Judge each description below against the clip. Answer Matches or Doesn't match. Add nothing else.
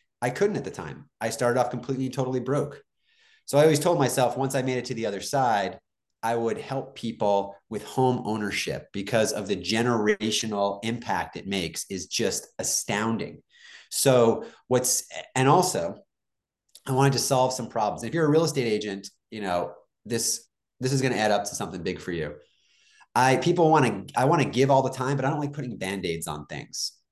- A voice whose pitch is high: Doesn't match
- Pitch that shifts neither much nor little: Matches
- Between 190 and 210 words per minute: Matches